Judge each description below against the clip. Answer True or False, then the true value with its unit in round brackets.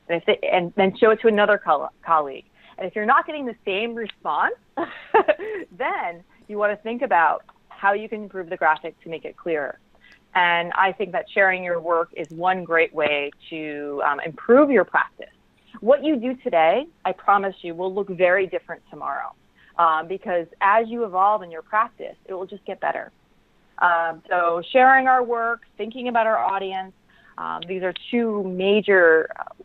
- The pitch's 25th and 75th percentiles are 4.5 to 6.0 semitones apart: True (4.9 semitones)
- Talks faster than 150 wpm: True (180 wpm)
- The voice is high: True (195 Hz)